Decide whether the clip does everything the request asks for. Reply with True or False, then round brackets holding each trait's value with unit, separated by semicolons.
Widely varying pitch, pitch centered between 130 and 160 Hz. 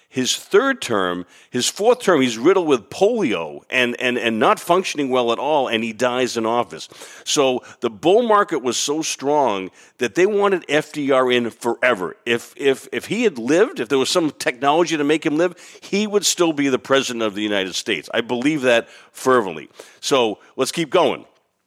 True (6.2 semitones; 135 Hz)